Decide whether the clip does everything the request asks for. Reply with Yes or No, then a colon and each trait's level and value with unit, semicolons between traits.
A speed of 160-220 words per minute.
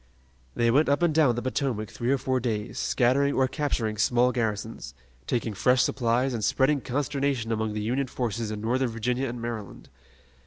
Yes: average, 180 wpm